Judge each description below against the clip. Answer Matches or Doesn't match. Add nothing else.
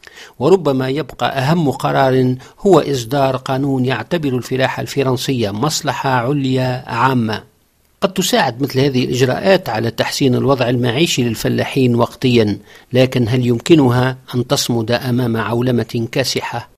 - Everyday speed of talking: Matches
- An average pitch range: Doesn't match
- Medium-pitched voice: Doesn't match